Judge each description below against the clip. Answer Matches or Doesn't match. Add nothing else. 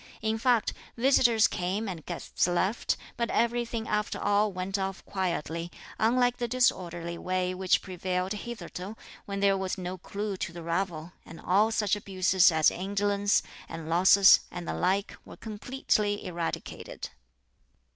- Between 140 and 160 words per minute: Matches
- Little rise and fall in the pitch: Doesn't match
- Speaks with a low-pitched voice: Doesn't match